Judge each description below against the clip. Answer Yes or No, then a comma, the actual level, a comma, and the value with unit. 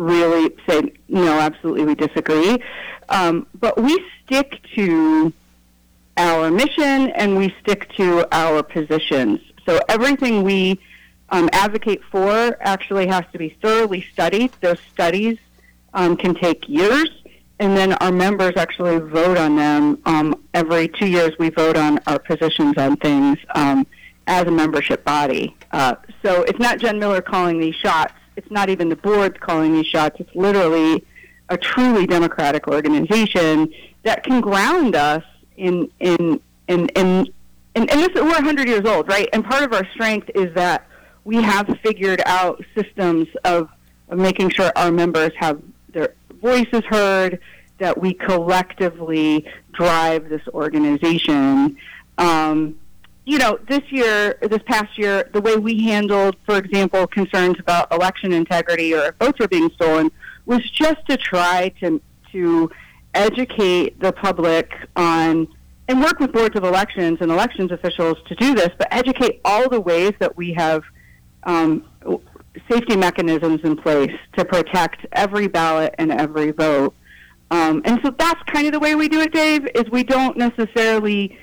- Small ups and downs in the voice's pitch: No, average, 5.2 semitones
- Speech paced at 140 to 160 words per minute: Yes, average, 155 wpm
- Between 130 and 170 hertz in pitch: No, medium, 185 Hz